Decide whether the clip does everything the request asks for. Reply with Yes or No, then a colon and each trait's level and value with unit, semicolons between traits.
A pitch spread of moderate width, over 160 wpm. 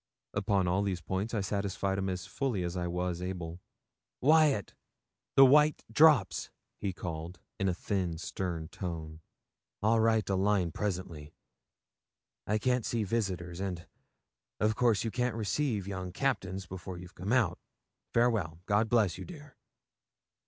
No: average, 4.0 semitones; average, 145 wpm